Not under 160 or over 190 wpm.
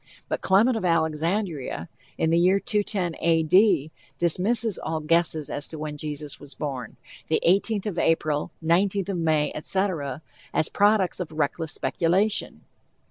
No: average, 145 wpm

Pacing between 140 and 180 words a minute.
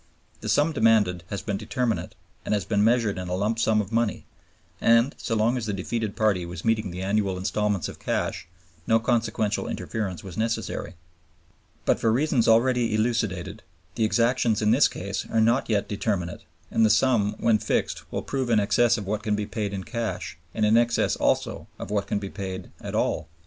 No: average, 195 wpm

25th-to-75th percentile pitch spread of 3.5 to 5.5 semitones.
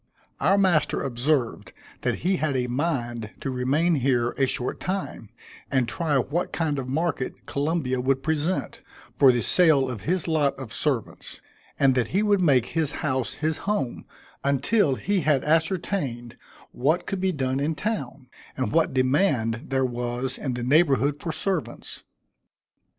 Yes: average, 4.3 semitones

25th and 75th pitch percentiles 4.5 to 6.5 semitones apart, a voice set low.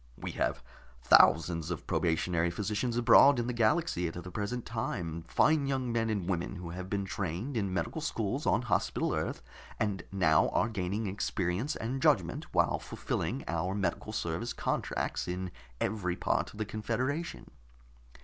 Yes: average, 4.9 semitones; low, 100 Hz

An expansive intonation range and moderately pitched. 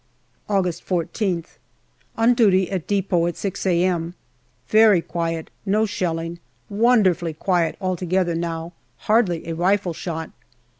No: average, 2.9 semitones; medium, 180 Hz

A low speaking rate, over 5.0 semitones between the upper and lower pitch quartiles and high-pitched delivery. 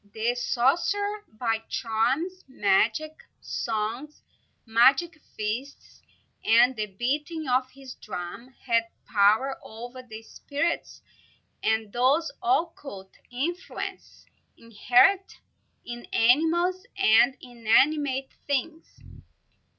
Yes: slow, 90 wpm; wide, 5.4 semitones; very high, 255 Hz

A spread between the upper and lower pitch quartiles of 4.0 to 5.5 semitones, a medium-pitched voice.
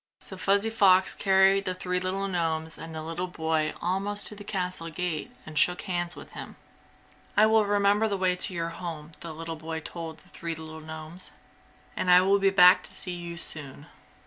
No: average, 3.0 semitones; medium, 180 Hz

